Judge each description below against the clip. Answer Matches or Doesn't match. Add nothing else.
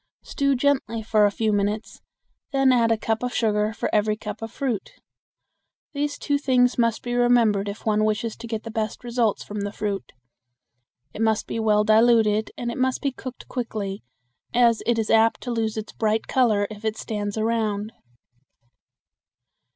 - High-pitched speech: Matches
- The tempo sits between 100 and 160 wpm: Doesn't match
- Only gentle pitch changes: Matches